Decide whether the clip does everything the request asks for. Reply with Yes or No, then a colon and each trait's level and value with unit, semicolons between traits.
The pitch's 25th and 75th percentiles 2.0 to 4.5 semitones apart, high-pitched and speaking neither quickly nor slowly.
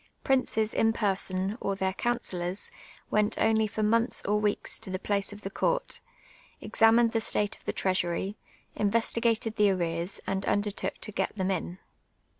Yes: average, 2.7 semitones; high, 205 Hz; average, 160 wpm